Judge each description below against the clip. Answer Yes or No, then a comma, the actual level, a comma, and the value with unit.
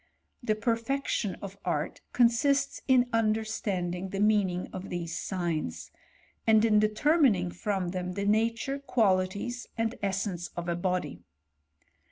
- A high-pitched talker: Yes, high, 205 Hz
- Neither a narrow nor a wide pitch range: Yes, average, 4.0 semitones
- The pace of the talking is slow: Yes, slow, 130 wpm